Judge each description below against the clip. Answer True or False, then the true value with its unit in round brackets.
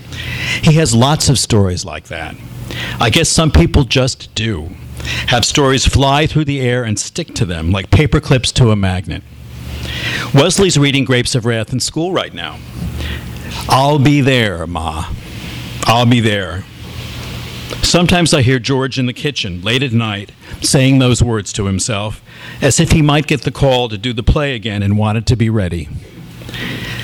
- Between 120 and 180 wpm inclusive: True (170 wpm)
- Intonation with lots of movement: True (6.1 semitones)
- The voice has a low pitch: True (120 Hz)